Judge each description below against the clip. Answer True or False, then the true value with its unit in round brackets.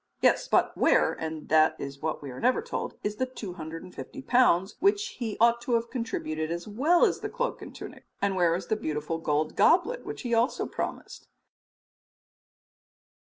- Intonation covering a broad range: True (7.9 semitones)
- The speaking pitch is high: True (205 Hz)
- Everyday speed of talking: True (180 wpm)